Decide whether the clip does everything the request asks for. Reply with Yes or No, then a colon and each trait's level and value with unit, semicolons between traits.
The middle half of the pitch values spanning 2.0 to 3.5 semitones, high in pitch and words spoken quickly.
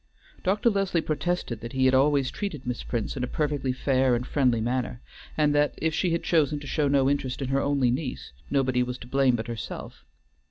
No: average, 2.9 semitones; low, 135 Hz; fast, 210 wpm